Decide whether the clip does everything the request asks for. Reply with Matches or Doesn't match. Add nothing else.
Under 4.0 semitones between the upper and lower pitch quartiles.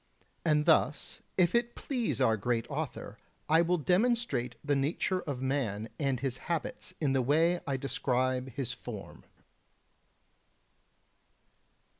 Doesn't match